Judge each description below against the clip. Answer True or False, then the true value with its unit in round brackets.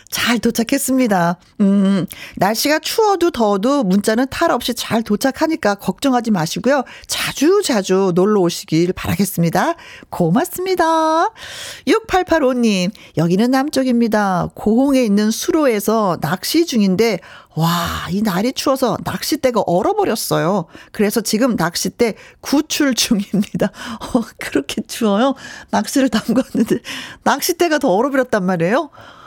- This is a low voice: False (235 Hz)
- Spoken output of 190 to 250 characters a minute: False (285 characters per minute)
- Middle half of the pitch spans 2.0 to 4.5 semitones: False (5.5 semitones)